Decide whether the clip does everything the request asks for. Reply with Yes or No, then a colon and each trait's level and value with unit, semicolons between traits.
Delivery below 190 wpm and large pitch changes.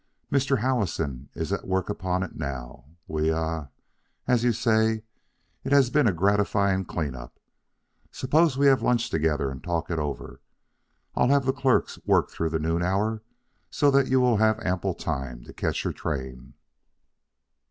Yes: average, 165 wpm; wide, 7.8 semitones